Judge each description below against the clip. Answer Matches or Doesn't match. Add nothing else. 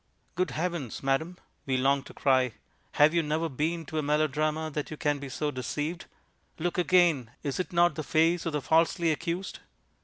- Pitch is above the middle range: Doesn't match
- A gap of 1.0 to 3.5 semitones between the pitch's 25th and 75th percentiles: Matches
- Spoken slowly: Doesn't match